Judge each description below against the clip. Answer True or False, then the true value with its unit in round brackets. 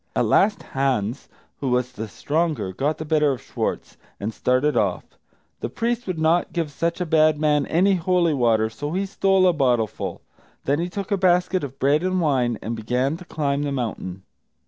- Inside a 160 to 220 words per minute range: True (190 wpm)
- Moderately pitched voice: True (150 Hz)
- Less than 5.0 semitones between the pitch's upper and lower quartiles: False (5.6 semitones)